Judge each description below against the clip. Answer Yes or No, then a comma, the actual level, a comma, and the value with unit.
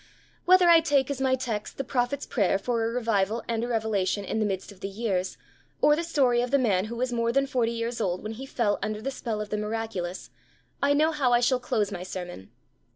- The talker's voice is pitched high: Yes, high, 230 Hz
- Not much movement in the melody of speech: No, average, 3.9 semitones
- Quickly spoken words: Yes, fast, 235 wpm